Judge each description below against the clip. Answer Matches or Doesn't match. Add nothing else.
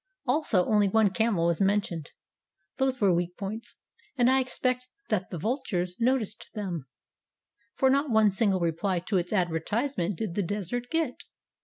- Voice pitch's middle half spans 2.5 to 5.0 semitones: Doesn't match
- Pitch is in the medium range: Doesn't match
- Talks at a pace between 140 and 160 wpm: Matches